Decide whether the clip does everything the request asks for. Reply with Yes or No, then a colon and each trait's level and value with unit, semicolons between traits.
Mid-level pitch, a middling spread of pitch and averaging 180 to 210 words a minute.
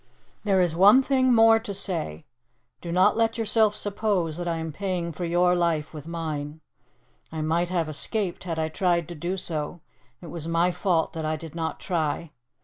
Yes: medium, 175 Hz; average, 3.4 semitones; average, 190 wpm